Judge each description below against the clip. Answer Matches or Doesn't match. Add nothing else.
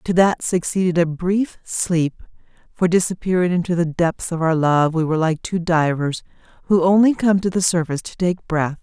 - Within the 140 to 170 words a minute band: Doesn't match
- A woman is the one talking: Matches